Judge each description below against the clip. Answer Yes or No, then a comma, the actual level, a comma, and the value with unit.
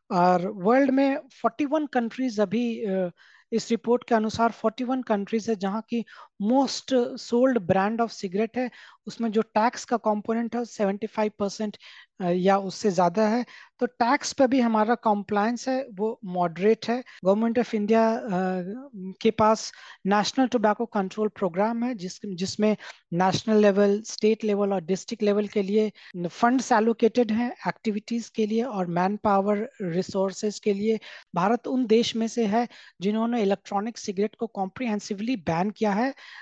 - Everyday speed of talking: Yes, average, 150 wpm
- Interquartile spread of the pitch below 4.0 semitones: Yes, average, 2.8 semitones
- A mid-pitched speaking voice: No, high, 220 Hz